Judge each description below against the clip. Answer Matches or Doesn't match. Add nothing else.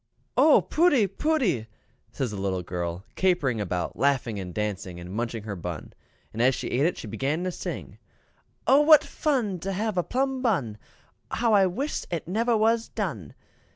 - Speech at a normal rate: Matches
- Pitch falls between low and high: Matches